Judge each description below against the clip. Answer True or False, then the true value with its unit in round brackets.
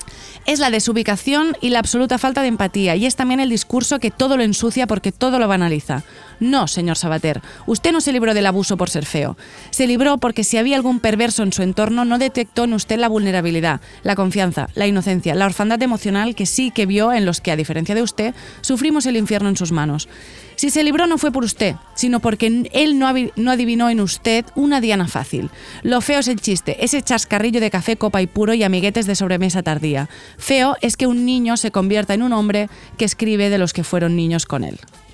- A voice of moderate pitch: False (220 Hz)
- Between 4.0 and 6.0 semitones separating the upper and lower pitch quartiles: True (4.6 semitones)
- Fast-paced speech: True (215 wpm)